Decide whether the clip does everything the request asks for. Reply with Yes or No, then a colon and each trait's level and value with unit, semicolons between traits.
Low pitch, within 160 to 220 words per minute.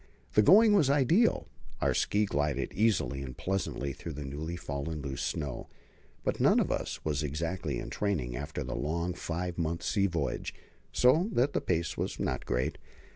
Yes: very low, 85 Hz; average, 175 wpm